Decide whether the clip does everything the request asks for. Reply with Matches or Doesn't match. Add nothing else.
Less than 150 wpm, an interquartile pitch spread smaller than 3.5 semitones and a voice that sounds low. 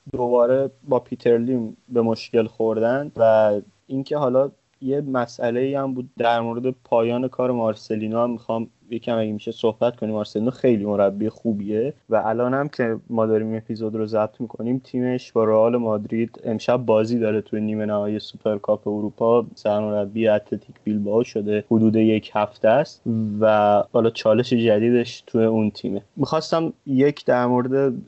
Doesn't match